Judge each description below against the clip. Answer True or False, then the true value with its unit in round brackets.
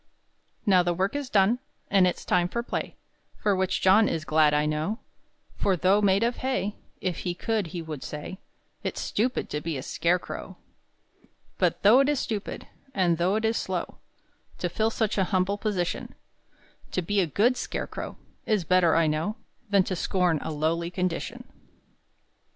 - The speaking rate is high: False (175 wpm)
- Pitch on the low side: False (185 Hz)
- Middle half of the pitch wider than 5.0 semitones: False (3.9 semitones)